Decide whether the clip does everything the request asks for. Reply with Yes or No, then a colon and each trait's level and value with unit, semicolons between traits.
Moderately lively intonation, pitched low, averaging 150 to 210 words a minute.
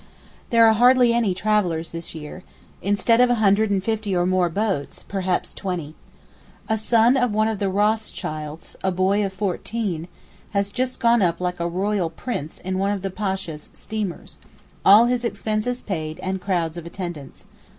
No: average, 3.7 semitones; high, 195 Hz; average, 170 wpm